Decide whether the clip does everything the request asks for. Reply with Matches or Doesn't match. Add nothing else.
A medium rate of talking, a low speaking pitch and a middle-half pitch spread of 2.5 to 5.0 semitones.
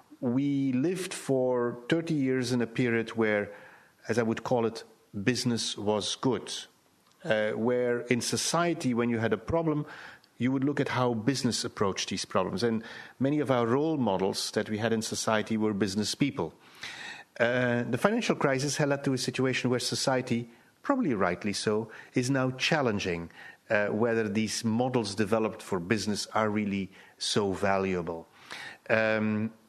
Matches